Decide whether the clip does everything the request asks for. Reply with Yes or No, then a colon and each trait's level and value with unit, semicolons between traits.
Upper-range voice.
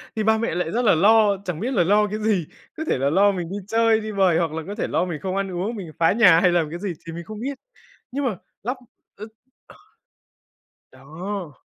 Yes: high, 195 Hz